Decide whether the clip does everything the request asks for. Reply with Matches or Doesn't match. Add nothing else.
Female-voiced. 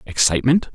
Doesn't match